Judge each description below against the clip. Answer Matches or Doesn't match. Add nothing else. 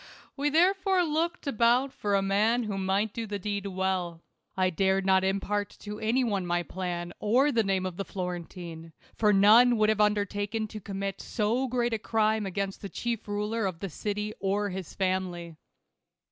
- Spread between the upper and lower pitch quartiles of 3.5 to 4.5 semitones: Doesn't match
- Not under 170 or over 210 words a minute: Matches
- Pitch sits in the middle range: Doesn't match